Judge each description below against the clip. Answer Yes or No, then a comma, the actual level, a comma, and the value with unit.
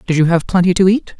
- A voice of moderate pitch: Yes, medium, 180 Hz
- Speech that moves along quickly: Yes, fast, 300 wpm